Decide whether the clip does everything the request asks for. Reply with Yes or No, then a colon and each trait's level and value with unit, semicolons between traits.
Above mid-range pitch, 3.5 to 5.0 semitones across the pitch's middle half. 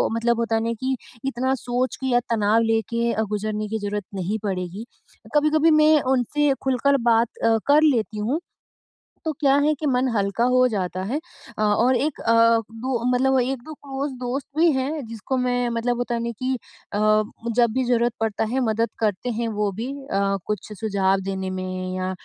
Yes: high, 235 Hz; average, 3.9 semitones